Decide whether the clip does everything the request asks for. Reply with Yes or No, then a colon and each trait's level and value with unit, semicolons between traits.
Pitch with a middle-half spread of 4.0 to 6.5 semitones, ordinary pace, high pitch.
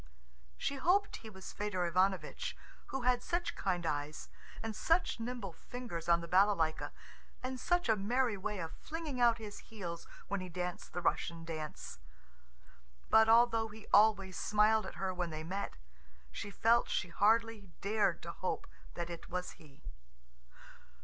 Yes: average, 4.7 semitones; average, 155 wpm; high, 205 Hz